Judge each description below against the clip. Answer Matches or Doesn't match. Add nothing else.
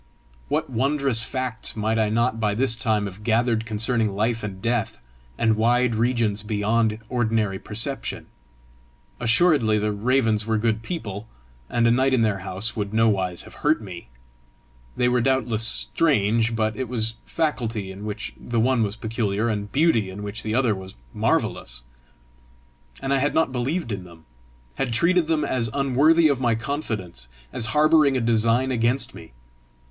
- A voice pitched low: Matches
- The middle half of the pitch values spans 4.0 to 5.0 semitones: Doesn't match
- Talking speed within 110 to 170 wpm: Matches